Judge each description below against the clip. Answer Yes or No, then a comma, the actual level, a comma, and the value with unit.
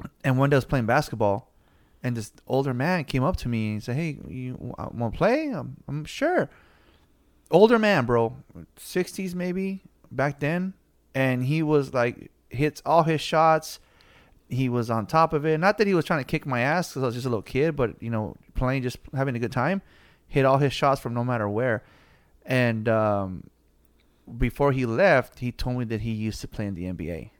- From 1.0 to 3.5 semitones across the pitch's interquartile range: No, average, 5.2 semitones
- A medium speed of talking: No, fast, 210 wpm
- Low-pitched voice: Yes, low, 130 Hz